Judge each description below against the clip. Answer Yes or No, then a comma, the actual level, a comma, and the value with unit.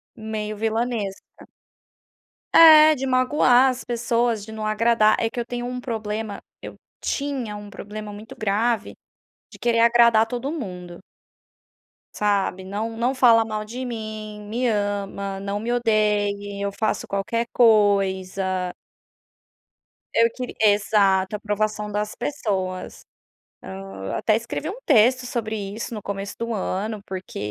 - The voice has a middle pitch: No, high, 215 Hz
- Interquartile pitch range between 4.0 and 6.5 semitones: No, average, 2.7 semitones